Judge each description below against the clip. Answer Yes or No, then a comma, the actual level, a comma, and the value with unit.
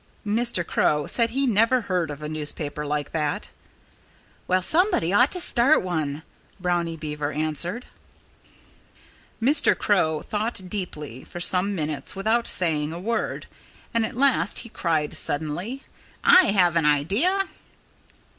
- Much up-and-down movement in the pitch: Yes, wide, 7.1 semitones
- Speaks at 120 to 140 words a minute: Yes, slow, 135 wpm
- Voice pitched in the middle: Yes, medium, 180 Hz